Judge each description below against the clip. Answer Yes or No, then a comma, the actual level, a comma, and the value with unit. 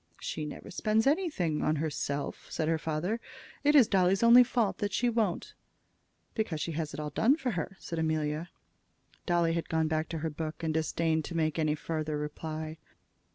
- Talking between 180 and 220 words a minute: Yes, average, 185 wpm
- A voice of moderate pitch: Yes, medium, 160 Hz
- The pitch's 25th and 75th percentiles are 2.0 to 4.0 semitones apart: No, average, 4.6 semitones